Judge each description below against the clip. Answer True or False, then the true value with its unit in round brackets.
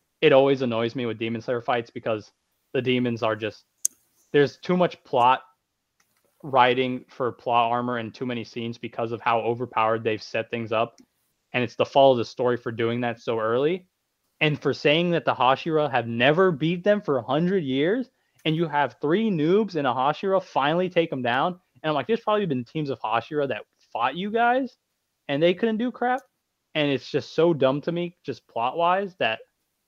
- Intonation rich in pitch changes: True (6.4 semitones)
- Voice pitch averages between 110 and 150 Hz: True (140 Hz)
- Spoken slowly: False (200 wpm)